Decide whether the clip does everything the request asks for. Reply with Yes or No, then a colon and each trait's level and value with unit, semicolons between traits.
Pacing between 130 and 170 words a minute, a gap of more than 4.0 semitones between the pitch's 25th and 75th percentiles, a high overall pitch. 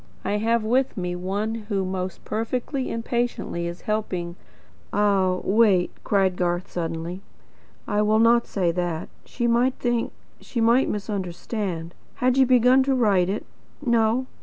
Yes: average, 145 wpm; average, 4.5 semitones; high, 210 Hz